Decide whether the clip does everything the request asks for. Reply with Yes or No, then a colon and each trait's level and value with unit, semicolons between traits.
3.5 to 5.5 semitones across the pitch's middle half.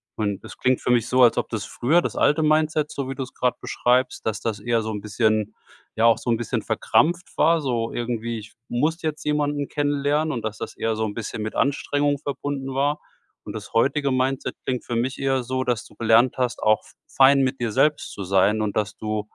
Yes: average, 4.3 semitones